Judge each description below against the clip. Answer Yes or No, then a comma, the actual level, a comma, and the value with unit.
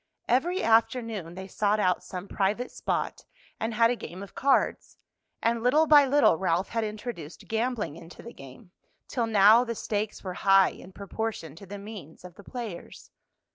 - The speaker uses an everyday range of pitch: Yes, average, 3.9 semitones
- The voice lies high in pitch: Yes, high, 215 Hz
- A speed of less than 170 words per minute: No, average, 175 wpm